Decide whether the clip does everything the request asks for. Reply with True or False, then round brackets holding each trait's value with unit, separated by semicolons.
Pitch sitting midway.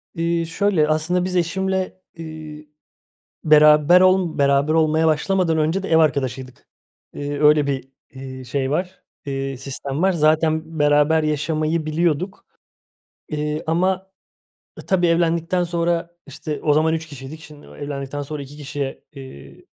True (155 Hz)